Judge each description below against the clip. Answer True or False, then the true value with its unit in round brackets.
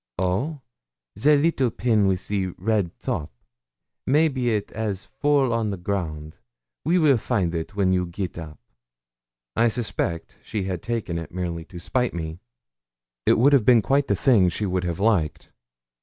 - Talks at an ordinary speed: True (165 wpm)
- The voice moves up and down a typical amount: False (5.7 semitones)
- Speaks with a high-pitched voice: False (100 Hz)